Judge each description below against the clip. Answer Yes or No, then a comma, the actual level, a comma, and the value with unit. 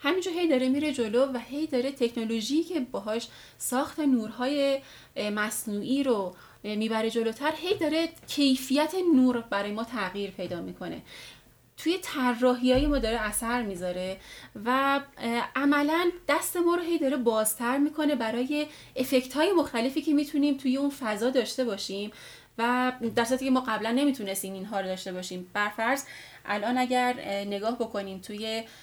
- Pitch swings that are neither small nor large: Yes, average, 4.5 semitones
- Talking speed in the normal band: Yes, average, 145 wpm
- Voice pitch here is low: No, very high, 250 Hz